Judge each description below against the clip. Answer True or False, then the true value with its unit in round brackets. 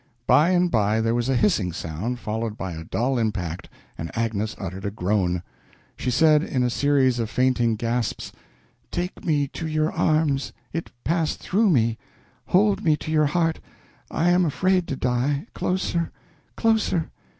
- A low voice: True (130 Hz)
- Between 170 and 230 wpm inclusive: False (160 wpm)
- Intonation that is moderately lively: False (6.6 semitones)